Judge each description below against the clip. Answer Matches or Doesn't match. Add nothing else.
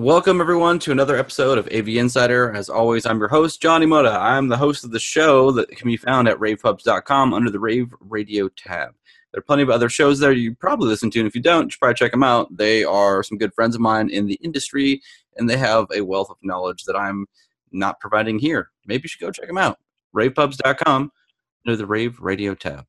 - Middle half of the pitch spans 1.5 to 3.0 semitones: Doesn't match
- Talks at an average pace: Doesn't match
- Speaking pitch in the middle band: Doesn't match